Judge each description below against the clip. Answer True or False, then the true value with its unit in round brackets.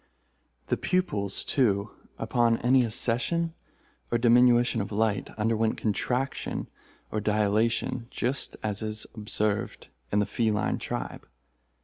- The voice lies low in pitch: True (115 Hz)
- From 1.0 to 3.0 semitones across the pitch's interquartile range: True (2.5 semitones)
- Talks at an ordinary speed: False (115 wpm)